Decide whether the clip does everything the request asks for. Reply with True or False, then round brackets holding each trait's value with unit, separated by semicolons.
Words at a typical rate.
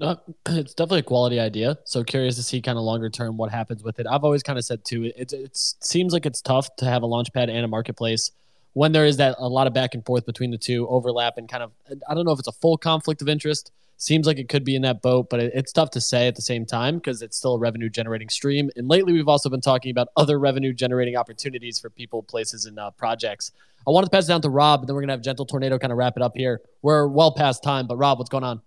False (290 wpm)